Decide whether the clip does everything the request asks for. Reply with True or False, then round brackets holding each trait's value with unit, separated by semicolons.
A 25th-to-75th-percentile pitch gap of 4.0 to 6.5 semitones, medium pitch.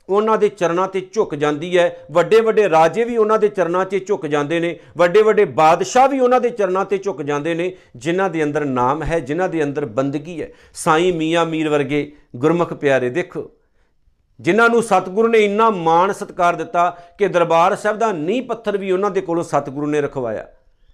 True (4.8 semitones; 175 Hz)